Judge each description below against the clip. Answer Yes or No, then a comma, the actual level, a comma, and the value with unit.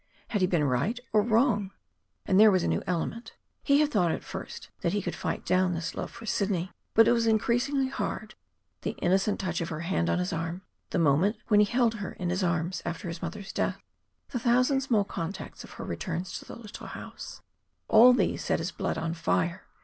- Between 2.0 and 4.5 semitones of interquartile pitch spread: No, average, 5.2 semitones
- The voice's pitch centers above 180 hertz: Yes, high, 190 Hz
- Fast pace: Yes, fast, 220 wpm